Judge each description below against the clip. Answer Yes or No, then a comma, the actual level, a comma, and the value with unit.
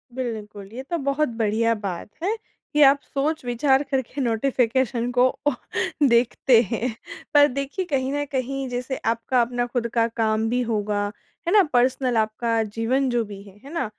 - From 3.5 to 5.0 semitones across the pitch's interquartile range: No, average, 3.1 semitones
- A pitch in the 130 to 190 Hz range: No, high, 245 Hz